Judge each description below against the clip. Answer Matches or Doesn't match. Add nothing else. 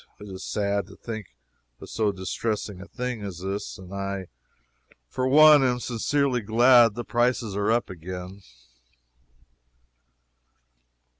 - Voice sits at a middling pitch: Doesn't match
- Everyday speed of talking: Doesn't match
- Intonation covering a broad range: Doesn't match